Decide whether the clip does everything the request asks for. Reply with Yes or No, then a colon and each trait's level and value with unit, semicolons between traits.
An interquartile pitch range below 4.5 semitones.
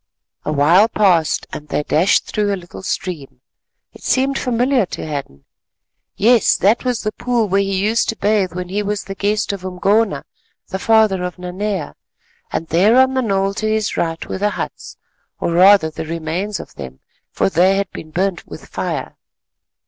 Yes: average, 3.7 semitones